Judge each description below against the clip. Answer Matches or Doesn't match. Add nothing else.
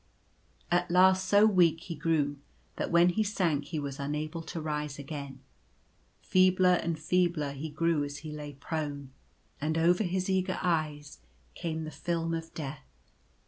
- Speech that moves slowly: Doesn't match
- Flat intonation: Doesn't match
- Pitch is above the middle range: Doesn't match